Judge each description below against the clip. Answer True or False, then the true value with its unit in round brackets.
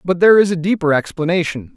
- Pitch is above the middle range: False (170 Hz)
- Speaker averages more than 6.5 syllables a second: True (6.7 syllables/s)